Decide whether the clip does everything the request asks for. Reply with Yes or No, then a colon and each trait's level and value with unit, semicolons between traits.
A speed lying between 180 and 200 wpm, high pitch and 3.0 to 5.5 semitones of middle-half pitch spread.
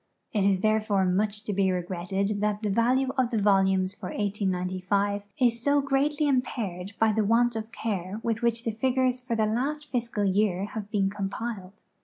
Yes: average, 185 wpm; high, 210 Hz; average, 3.3 semitones